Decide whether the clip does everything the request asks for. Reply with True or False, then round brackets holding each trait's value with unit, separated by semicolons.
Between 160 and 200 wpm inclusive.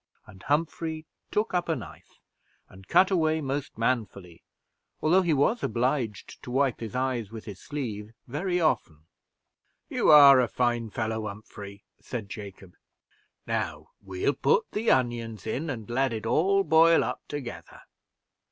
False (145 wpm)